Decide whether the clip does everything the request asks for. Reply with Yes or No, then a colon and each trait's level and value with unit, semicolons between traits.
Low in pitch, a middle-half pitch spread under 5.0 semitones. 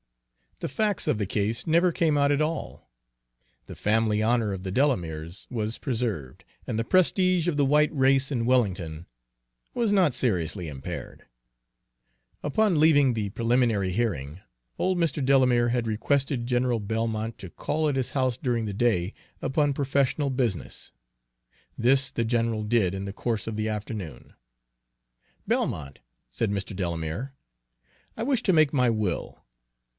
No: low, 120 Hz; wide, 5.4 semitones